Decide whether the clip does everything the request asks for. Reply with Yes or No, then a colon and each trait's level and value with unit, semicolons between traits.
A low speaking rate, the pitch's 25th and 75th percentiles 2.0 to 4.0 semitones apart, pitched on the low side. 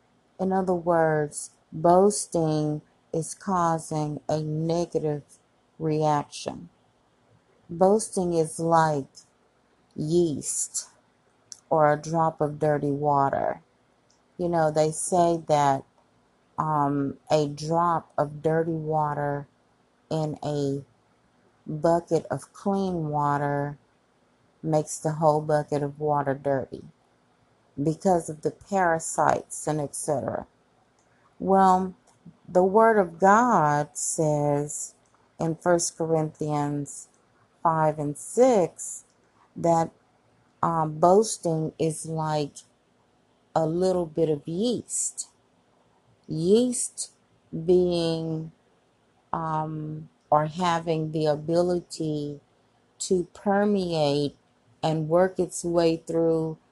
No: slow, 90 wpm; narrow, 2.6 semitones; medium, 160 Hz